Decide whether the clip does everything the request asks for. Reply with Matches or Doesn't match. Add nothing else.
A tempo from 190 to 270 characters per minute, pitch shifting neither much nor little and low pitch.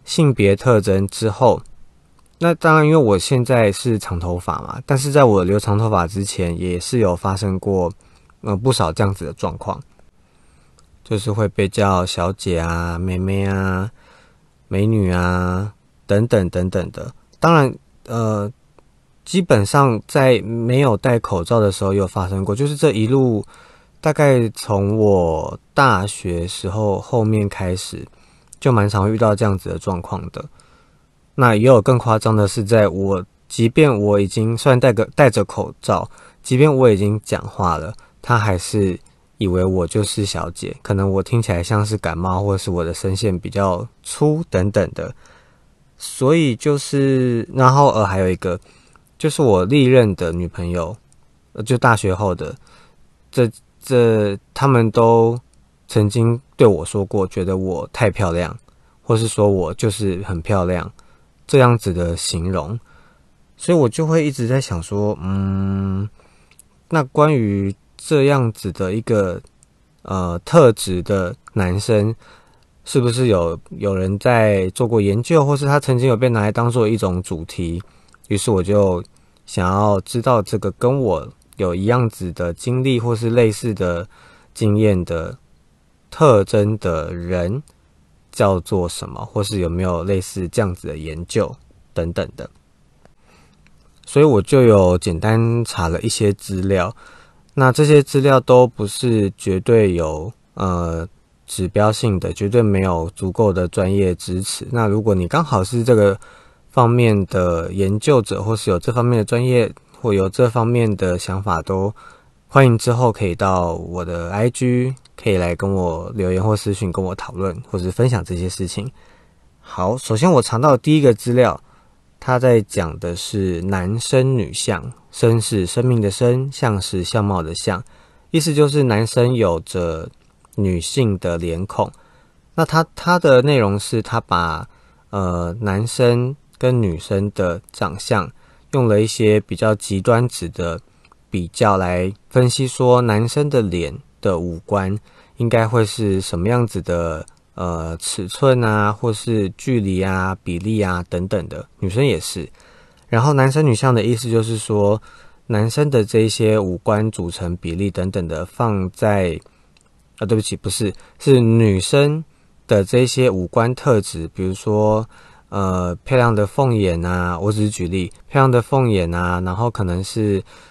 Matches